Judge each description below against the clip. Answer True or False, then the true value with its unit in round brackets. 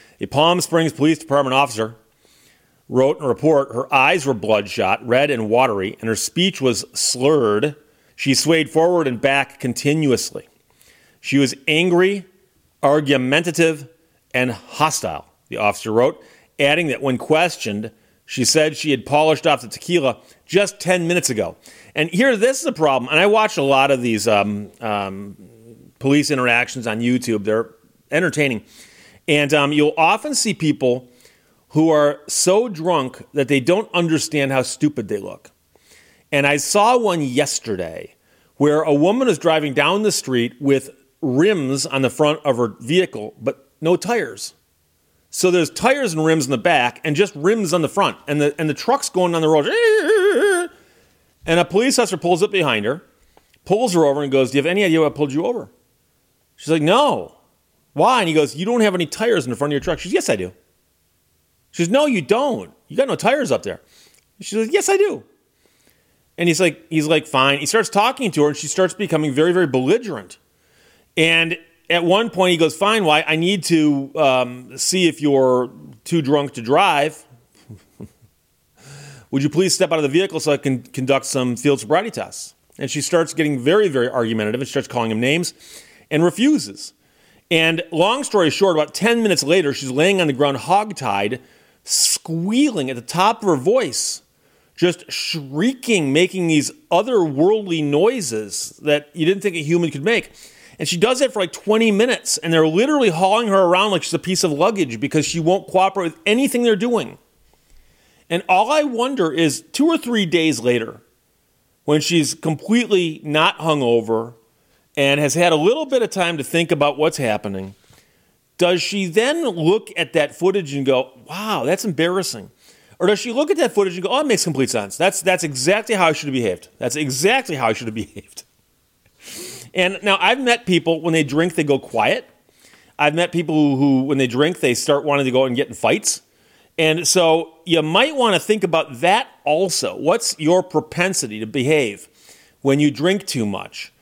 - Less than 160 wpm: False (185 wpm)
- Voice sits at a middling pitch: True (155 Hz)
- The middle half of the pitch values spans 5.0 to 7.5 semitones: True (5.3 semitones)